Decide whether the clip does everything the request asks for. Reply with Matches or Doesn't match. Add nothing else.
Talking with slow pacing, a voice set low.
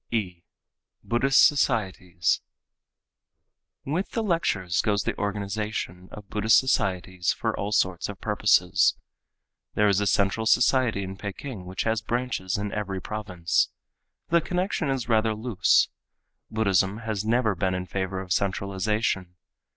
Matches